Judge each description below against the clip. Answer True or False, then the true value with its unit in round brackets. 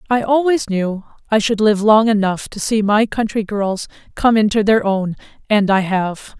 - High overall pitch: True (210 Hz)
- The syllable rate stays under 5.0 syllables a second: True (4.5 syllables/s)